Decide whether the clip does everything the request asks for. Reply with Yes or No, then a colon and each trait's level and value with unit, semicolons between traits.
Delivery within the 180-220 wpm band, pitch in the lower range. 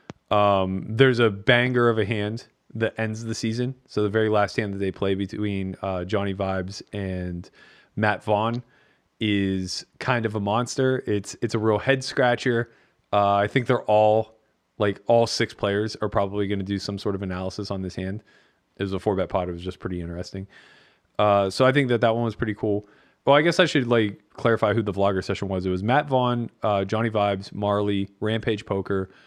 Yes: fast, 205 wpm; low, 105 Hz